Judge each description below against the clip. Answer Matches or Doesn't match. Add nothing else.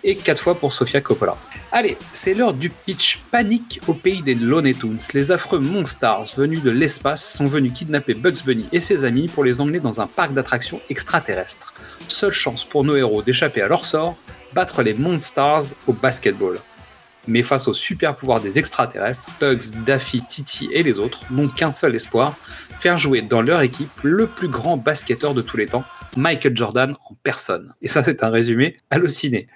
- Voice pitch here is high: Doesn't match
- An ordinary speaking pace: Matches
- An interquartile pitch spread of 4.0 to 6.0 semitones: Matches